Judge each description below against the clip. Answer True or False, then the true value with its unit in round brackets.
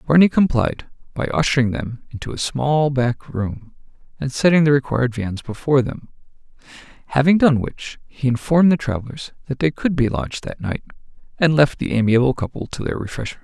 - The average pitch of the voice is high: False (135 Hz)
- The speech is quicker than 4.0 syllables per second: True (5.5 syllables/s)